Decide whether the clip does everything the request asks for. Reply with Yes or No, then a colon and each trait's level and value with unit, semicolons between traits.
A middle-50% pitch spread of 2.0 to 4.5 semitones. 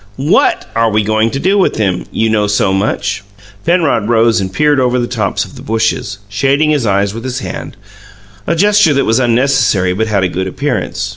No: average, 5.0 semitones